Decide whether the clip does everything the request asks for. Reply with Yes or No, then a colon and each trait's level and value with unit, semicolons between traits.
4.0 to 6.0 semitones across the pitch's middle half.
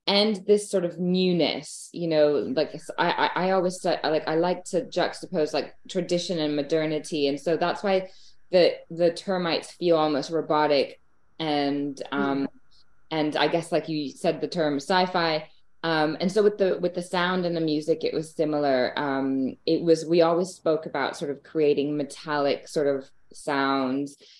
No: average, 3.3 semitones